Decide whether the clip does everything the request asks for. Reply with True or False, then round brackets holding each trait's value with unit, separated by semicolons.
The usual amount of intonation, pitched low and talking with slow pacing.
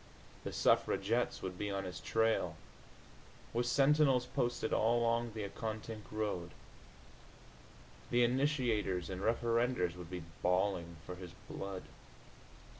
True (4.5 semitones; 110 Hz; 115 wpm)